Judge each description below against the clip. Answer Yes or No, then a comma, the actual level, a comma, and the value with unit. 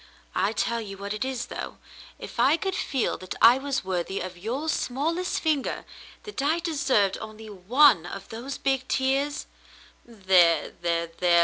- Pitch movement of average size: No, wide, 6.5 semitones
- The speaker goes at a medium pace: Yes, average, 185 wpm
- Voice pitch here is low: No, high, 235 Hz